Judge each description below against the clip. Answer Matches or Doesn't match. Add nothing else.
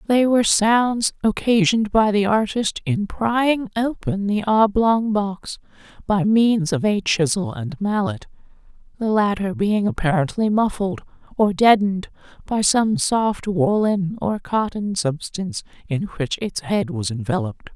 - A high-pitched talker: Matches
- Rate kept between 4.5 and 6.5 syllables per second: Doesn't match